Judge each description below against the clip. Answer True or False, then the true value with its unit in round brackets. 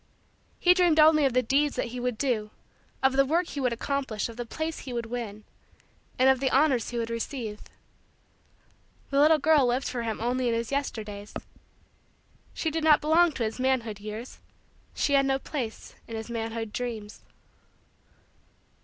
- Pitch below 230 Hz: False (250 Hz)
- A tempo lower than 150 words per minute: False (175 wpm)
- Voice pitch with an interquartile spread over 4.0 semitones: False (3.7 semitones)